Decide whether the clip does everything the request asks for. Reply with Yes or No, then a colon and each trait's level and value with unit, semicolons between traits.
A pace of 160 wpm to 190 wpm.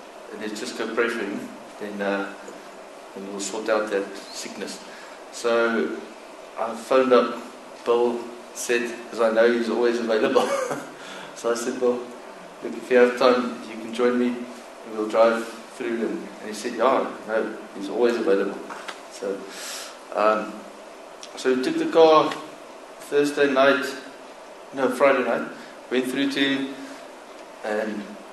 No: average, 140 wpm